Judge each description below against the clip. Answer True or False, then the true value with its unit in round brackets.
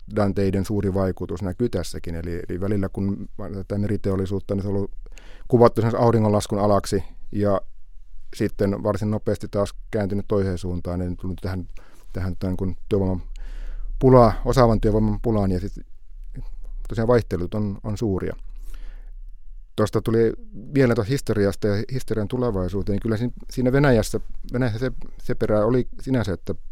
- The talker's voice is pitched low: True (100 Hz)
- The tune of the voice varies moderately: True (3.4 semitones)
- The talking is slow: False (140 wpm)